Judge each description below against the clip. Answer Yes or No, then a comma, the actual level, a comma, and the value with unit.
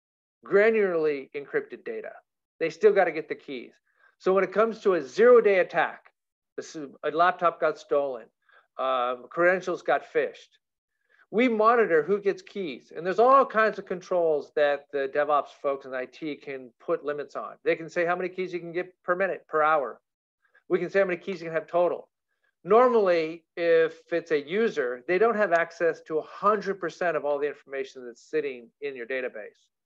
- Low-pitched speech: No, medium, 180 Hz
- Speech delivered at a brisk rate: No, average, 185 wpm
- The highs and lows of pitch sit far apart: Yes, wide, 6.6 semitones